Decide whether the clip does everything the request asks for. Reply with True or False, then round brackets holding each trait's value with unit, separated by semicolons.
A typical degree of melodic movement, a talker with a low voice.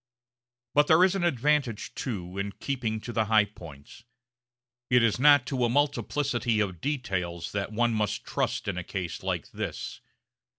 False (5.8 semitones; 115 Hz)